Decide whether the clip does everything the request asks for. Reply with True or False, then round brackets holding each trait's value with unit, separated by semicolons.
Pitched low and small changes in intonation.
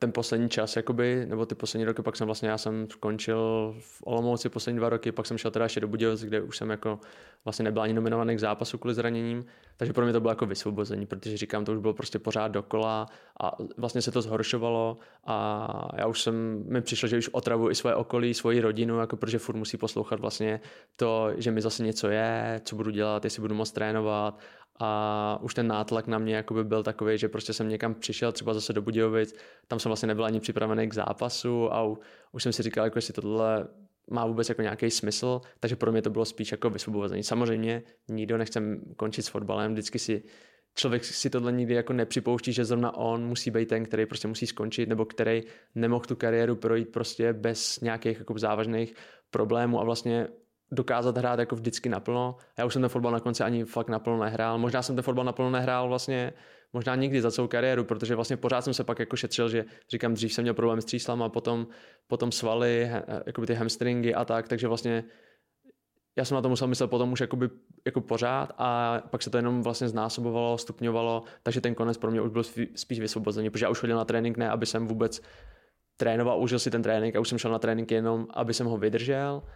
True (115 Hz; 1.5 semitones)